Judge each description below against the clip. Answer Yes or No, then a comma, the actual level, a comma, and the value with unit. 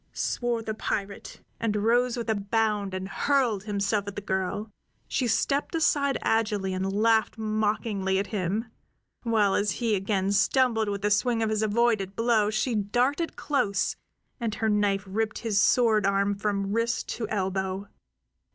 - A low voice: No, high, 210 Hz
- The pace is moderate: Yes, average, 160 wpm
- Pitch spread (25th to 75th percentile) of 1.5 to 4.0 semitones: Yes, narrow, 2.5 semitones